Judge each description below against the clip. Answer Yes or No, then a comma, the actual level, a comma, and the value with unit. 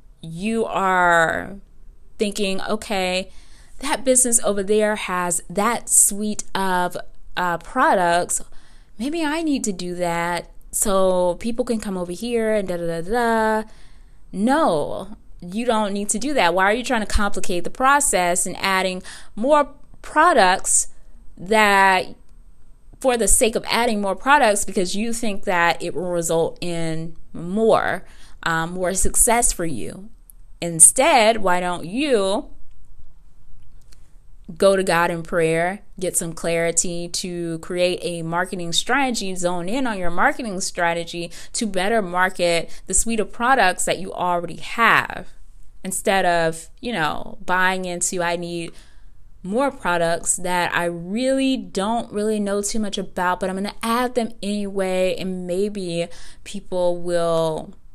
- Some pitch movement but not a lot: Yes, average, 3.9 semitones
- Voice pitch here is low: No, high, 190 Hz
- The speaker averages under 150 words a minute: Yes, average, 140 wpm